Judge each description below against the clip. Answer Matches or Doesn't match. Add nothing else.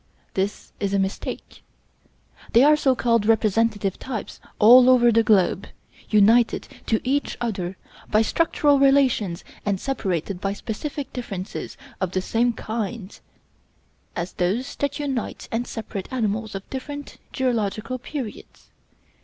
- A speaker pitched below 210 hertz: Doesn't match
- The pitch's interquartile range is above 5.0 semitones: Doesn't match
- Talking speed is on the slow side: Matches